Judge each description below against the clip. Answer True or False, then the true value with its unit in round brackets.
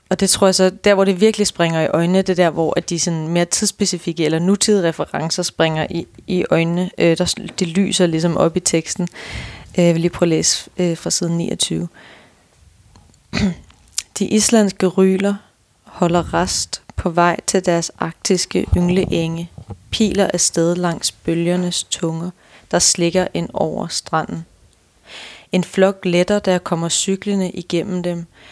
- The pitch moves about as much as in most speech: False (2.3 semitones)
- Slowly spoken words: False (160 wpm)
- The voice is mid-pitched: True (175 Hz)